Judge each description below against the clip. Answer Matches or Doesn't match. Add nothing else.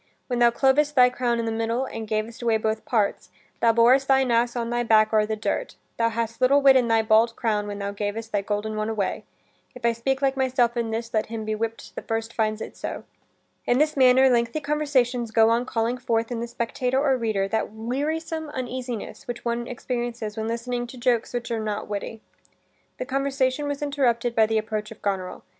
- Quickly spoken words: Matches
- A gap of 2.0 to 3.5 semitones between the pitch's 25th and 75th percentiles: Matches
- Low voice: Doesn't match